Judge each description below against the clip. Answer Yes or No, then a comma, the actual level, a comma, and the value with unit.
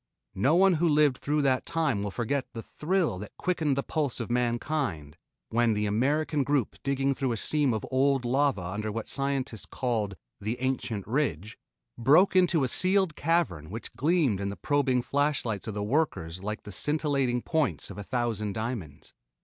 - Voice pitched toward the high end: No, low, 130 Hz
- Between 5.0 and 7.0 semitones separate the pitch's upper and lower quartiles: Yes, wide, 5.5 semitones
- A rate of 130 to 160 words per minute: No, average, 175 wpm